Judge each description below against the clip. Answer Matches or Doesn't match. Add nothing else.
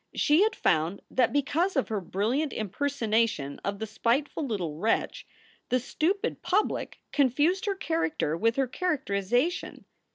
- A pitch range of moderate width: Doesn't match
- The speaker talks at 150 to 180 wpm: Doesn't match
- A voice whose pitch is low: Doesn't match